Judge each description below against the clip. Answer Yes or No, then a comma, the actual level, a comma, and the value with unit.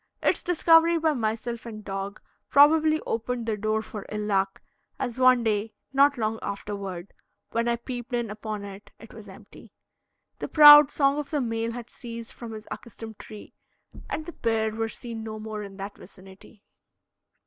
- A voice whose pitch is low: No, high, 225 Hz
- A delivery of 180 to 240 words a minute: No, average, 170 wpm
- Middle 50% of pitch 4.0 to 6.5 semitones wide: No, average, 3.1 semitones